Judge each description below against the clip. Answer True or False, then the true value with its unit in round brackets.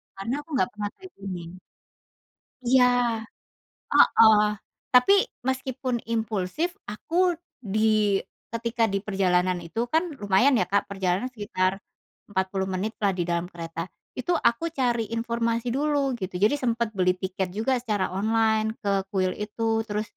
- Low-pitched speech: False (215 Hz)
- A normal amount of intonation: True (3.8 semitones)